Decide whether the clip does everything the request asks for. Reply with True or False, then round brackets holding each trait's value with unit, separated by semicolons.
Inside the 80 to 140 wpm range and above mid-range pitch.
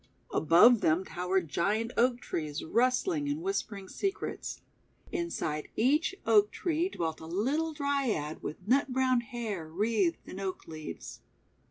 True (135 wpm; 225 Hz)